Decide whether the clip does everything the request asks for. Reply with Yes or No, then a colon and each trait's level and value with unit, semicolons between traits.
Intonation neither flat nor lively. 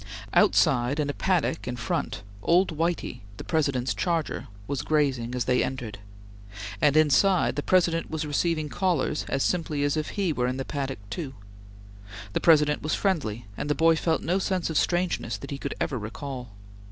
Yes: average, 4.1 semitones